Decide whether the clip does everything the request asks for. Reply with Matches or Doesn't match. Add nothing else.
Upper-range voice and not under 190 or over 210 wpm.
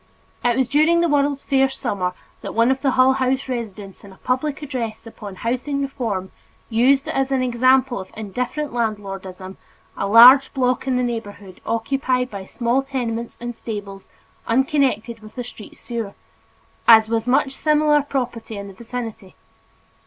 Doesn't match